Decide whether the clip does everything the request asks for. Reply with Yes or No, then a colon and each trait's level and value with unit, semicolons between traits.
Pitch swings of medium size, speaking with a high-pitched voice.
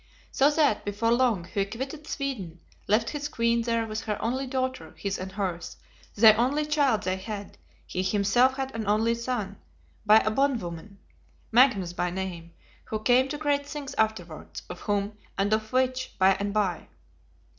Yes: average, 4.6 semitones; high, 220 Hz